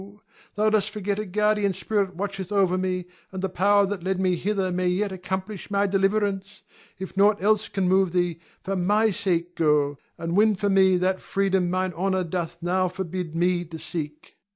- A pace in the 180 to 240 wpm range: Yes, average, 185 wpm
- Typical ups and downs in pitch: No, narrow, 2.0 semitones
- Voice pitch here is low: No, high, 190 Hz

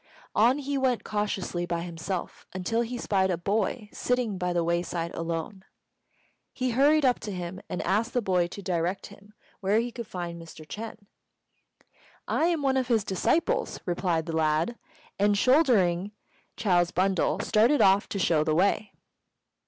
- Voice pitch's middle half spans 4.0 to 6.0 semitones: Yes, average, 5.1 semitones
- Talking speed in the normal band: Yes, average, 160 wpm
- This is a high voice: Yes, high, 195 Hz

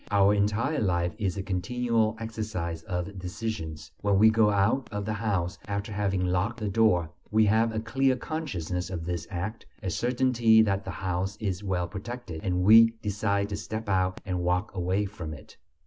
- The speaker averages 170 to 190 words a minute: Yes, average, 180 wpm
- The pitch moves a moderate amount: Yes, average, 3.5 semitones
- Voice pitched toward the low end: Yes, low, 100 Hz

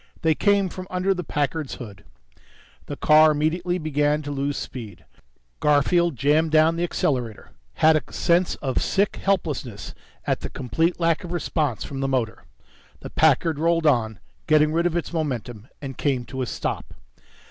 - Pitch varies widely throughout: No, average, 3.9 semitones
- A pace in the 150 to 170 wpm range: Yes, average, 165 wpm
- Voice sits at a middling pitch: Yes, medium, 155 Hz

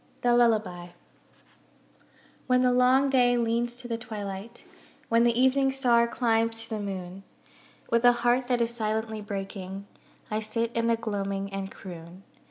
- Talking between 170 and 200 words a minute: No, average, 155 wpm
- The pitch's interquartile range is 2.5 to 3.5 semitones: Yes, average, 3.2 semitones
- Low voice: No, high, 230 Hz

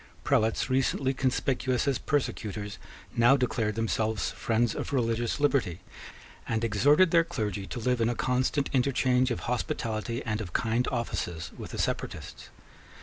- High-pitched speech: No, low, 120 Hz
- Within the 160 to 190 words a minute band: No, average, 145 wpm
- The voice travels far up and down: No, average, 3.1 semitones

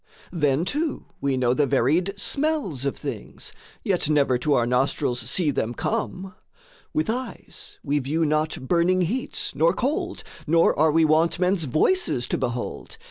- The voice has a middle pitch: Yes, medium, 160 Hz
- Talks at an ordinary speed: Yes, average, 155 wpm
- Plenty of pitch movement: Yes, wide, 5.8 semitones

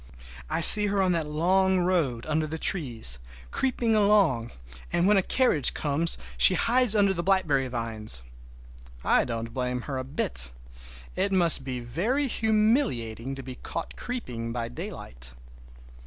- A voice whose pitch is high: No, medium, 155 Hz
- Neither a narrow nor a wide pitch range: No, wide, 8.5 semitones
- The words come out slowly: No, average, 150 wpm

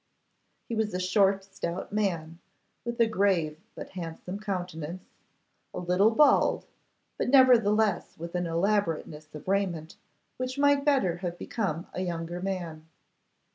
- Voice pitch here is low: No, medium, 185 Hz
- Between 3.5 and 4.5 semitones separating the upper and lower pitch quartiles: Yes, average, 4.0 semitones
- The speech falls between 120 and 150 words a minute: Yes, slow, 135 wpm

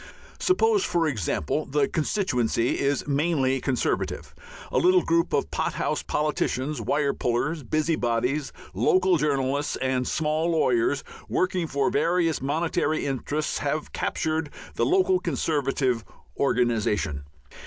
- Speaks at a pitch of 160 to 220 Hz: No, medium, 145 Hz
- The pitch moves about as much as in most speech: Yes, average, 4.0 semitones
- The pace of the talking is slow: Yes, slow, 110 wpm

